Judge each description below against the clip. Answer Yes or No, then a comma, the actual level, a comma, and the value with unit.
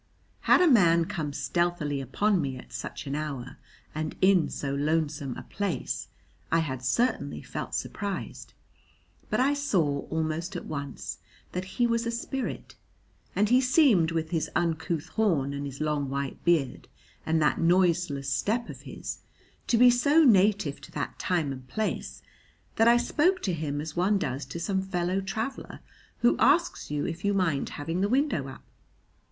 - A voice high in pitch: No, medium, 170 Hz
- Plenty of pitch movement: Yes, wide, 6.4 semitones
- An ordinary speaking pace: Yes, average, 170 wpm